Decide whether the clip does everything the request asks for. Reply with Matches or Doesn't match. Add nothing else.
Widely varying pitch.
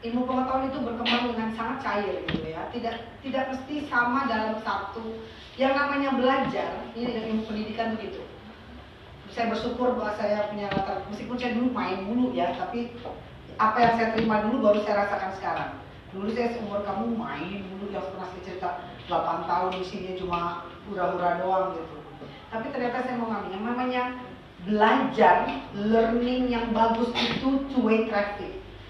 Doesn't match